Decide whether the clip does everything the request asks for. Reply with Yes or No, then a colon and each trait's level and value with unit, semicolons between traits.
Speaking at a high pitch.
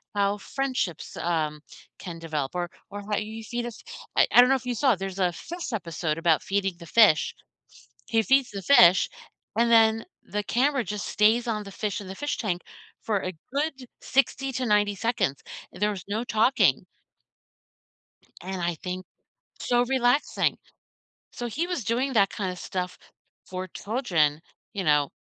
Yes: high, 210 Hz